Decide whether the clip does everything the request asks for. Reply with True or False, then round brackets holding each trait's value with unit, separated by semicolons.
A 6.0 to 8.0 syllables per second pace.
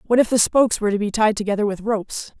True (7.4 syllables/s)